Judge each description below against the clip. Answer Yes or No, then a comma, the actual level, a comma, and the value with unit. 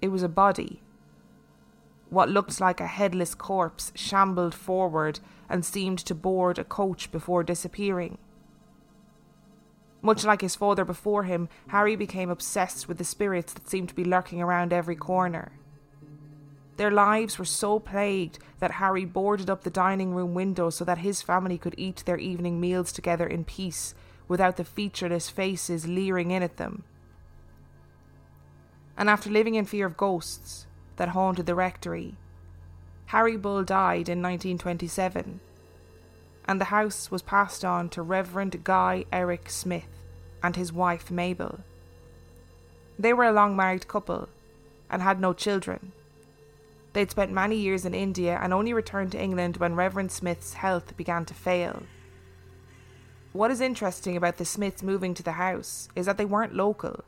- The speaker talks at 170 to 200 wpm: No, average, 155 wpm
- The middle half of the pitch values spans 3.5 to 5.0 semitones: Yes, average, 3.8 semitones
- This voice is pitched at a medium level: Yes, medium, 180 Hz